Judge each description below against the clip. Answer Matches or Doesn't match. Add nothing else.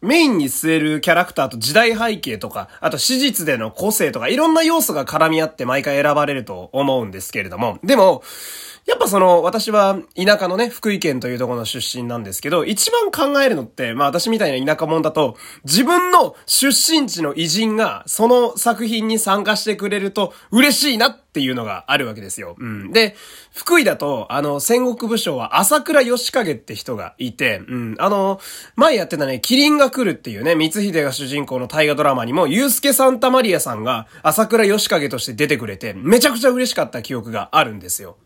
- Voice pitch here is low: Doesn't match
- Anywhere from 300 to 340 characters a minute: Doesn't match